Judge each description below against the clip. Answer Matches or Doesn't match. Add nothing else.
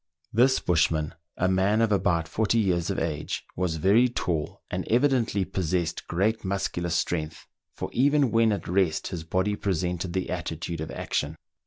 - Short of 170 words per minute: Matches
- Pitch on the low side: Matches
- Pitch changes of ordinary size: Matches